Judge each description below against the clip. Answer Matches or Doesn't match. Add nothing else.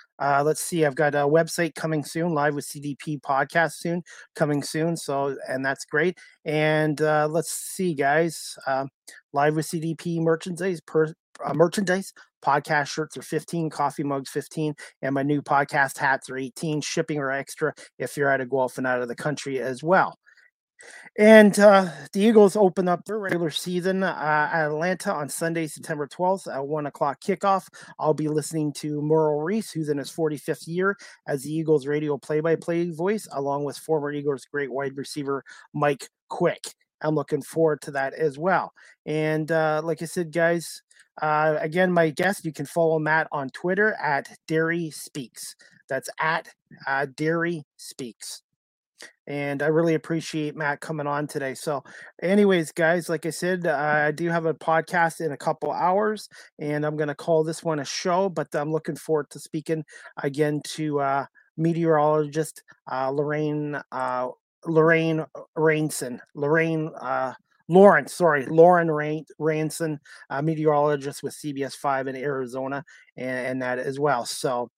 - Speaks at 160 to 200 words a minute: Matches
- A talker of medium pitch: Matches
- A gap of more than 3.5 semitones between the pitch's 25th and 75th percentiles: Doesn't match